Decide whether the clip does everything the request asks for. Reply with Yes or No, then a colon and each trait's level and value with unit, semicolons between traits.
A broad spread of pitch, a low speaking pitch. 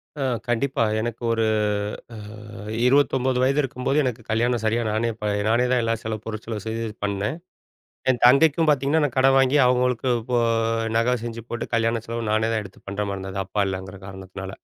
No: average, 2.9 semitones; low, 115 Hz